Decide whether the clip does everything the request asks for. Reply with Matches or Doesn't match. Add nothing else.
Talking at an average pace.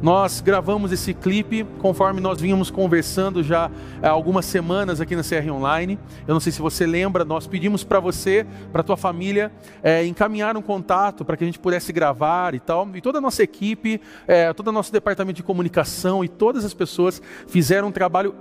Doesn't match